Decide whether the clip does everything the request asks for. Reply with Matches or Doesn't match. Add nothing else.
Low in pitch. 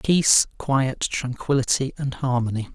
Matches